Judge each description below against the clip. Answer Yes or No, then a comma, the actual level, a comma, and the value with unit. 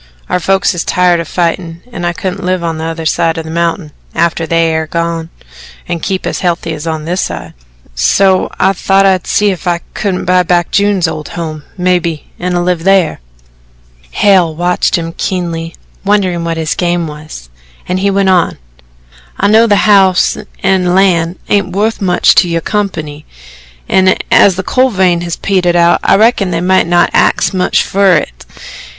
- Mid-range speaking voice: Yes, medium, 175 Hz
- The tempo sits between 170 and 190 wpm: Yes, average, 180 wpm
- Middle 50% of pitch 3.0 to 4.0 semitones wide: No, narrow, 2.4 semitones